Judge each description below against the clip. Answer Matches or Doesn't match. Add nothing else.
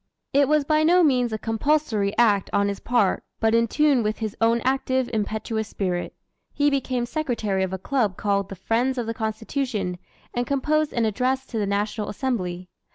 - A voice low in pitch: Doesn't match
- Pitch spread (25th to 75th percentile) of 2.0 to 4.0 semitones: Doesn't match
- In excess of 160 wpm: Matches